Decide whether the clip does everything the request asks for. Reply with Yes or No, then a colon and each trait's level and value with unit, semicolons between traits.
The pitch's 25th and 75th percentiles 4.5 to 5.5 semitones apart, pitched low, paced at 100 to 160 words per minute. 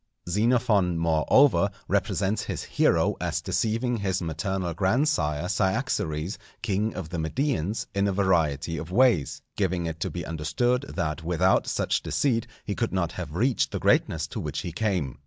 Yes: average, 5.2 semitones; very low, 95 Hz; average, 155 wpm